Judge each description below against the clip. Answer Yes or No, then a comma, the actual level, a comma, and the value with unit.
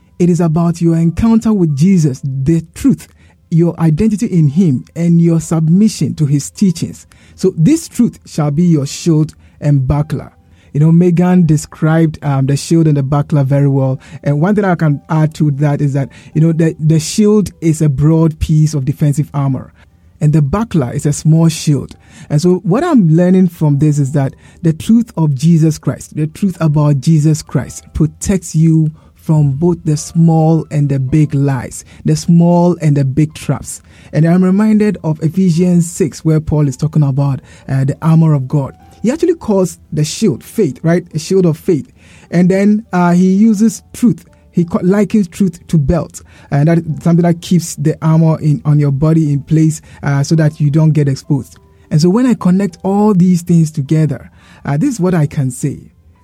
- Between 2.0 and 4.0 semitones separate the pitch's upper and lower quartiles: Yes, average, 3.3 semitones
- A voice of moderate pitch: Yes, medium, 160 Hz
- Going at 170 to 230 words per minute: Yes, average, 190 wpm